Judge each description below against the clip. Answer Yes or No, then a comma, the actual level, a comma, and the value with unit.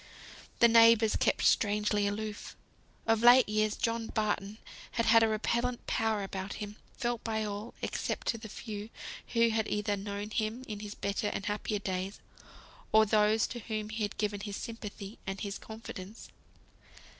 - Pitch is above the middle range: Yes, high, 215 Hz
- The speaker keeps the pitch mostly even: Yes, narrow, 1.6 semitones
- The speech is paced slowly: No, average, 165 wpm